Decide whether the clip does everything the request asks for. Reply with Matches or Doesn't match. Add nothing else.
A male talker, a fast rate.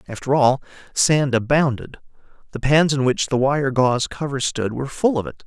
Doesn't match